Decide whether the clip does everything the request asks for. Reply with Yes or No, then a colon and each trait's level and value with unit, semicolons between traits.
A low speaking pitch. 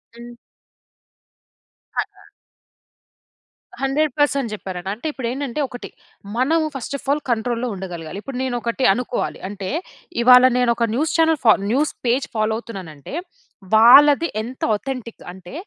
No: high, 245 Hz